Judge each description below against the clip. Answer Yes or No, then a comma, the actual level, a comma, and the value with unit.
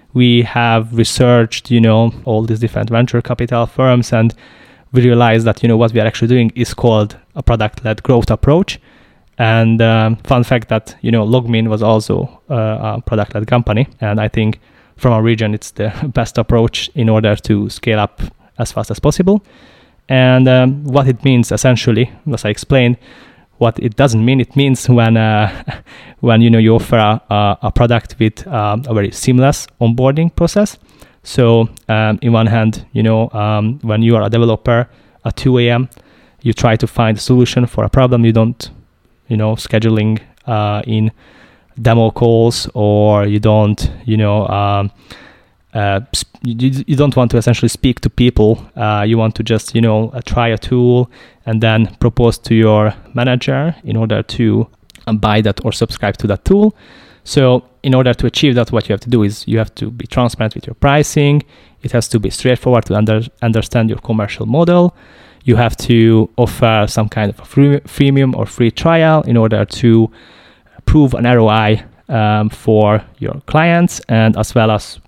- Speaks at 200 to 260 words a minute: No, average, 185 wpm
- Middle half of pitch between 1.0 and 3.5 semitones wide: Yes, narrow, 2.4 semitones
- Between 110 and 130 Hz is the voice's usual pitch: Yes, low, 115 Hz